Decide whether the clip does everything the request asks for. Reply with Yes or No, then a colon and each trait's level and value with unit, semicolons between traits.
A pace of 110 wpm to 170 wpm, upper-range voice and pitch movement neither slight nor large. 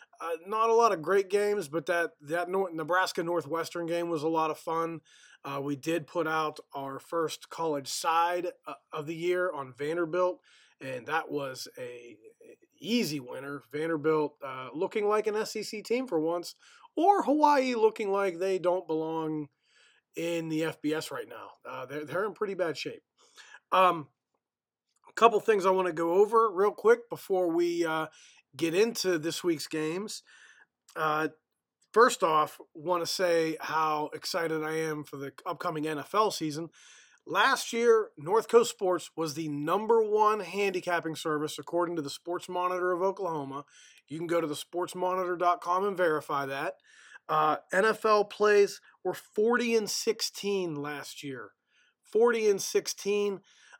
No: average, 160 wpm; medium, 175 Hz; average, 4.8 semitones